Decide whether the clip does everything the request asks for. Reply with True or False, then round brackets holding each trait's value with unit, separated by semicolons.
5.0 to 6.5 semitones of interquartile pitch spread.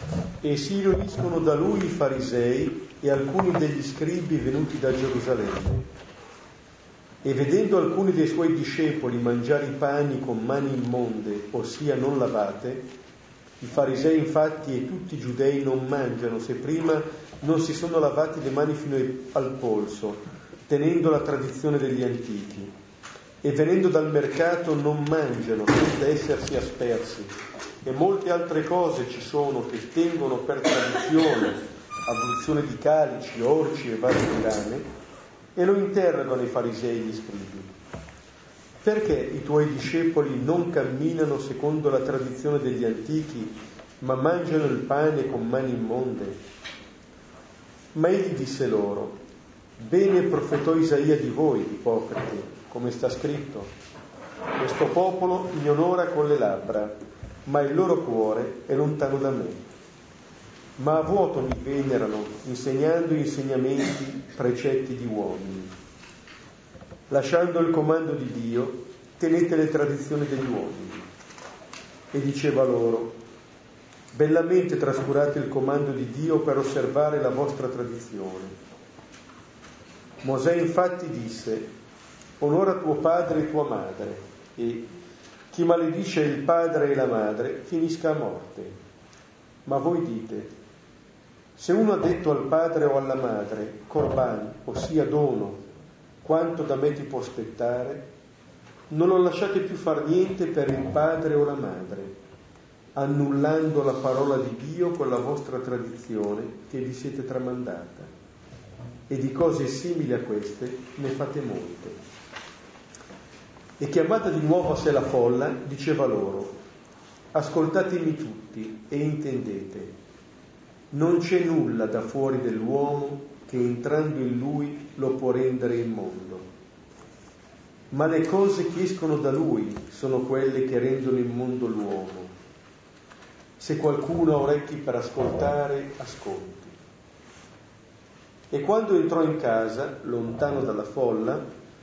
False (4.1 semitones)